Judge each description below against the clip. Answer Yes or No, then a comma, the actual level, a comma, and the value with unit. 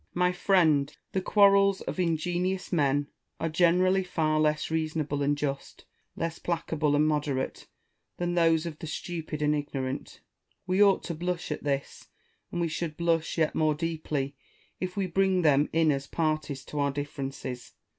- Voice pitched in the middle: Yes, medium, 160 Hz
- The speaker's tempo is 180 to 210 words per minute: No, average, 165 wpm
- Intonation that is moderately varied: Yes, average, 3.2 semitones